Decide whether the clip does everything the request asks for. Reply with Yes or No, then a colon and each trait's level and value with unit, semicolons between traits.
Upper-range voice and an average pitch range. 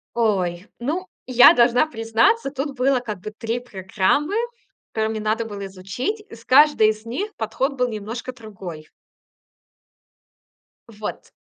Yes: high, 230 Hz; average, 3.5 semitones